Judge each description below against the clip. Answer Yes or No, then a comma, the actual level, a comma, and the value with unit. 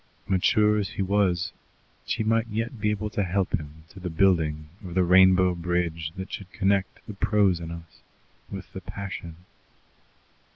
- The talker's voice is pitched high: No, very low, 95 Hz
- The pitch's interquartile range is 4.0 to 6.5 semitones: No, average, 2.8 semitones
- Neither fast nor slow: Yes, average, 165 wpm